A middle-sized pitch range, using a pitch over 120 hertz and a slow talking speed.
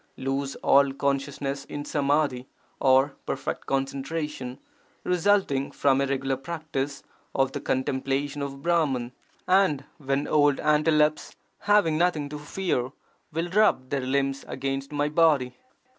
No: narrow, 2.1 semitones; medium, 140 Hz; slow, 130 wpm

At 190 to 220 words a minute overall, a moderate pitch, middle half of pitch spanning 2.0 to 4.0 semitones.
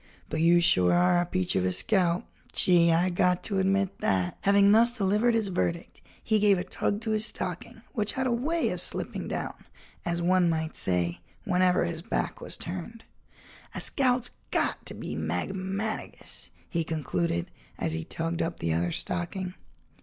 No: average, 170 wpm; medium, 180 Hz; average, 3.6 semitones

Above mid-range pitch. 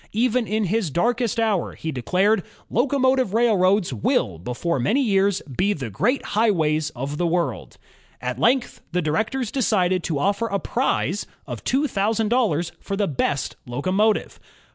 Yes: high, 200 Hz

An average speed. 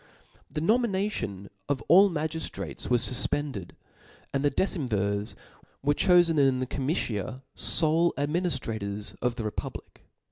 No: slow, 120 wpm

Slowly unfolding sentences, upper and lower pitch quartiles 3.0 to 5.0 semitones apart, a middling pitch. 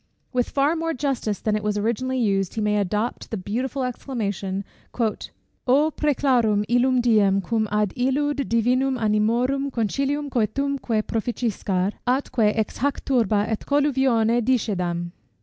No: slow, 130 wpm; average, 4.0 semitones; high, 235 Hz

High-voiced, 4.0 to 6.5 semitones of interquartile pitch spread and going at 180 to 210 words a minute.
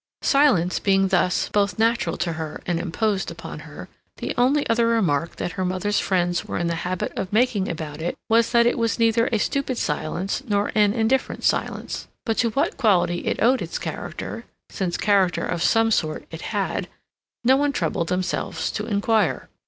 Yes: high, 205 Hz; average, 4.7 semitones; average, 185 wpm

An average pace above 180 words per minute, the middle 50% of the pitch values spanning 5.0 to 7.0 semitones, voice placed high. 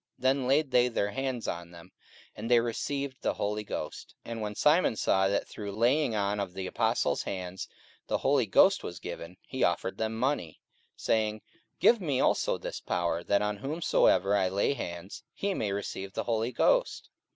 No: average, 190 wpm; average, 5.3 semitones; low, 105 Hz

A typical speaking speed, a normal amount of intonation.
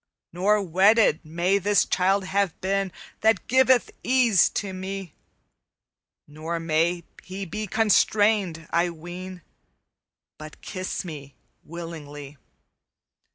No: slow, 105 wpm; average, 3.3 semitones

